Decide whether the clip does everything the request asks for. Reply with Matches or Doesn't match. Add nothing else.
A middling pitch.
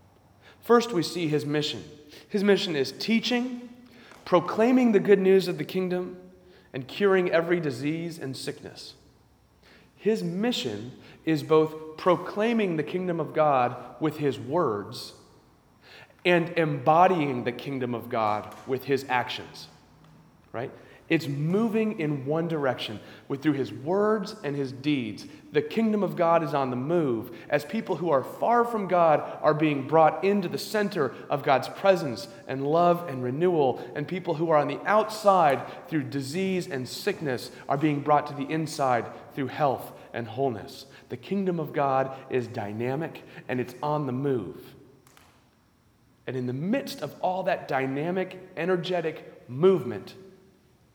Matches